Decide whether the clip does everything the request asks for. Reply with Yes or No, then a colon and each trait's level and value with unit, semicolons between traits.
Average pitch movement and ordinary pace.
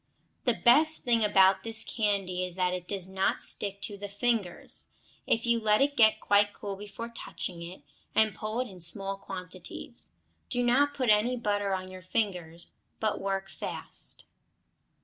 Yes: average, 3.4 semitones; average, 170 wpm